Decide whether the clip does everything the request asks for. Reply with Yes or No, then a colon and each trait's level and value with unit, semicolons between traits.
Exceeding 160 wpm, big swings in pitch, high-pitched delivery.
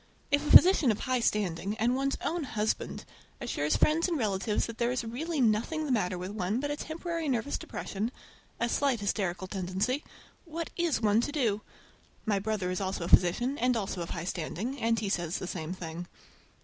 Yes: average, 185 wpm; wide, 6.4 semitones; high, 225 Hz